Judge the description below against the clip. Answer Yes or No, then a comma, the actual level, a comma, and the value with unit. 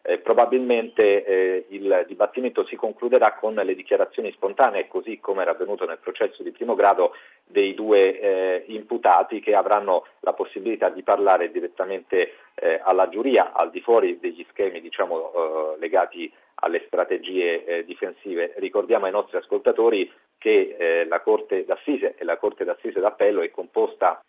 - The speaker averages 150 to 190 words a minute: Yes, average, 155 wpm